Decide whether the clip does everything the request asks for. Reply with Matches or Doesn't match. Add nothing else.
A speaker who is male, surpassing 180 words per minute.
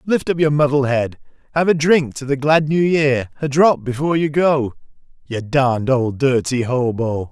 Matches